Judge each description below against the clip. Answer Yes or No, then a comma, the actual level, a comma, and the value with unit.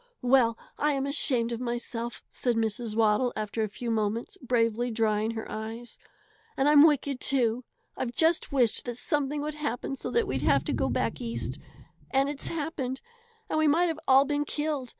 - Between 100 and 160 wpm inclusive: No, average, 180 wpm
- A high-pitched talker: Yes, very high, 250 Hz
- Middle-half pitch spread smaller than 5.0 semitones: Yes, average, 3.9 semitones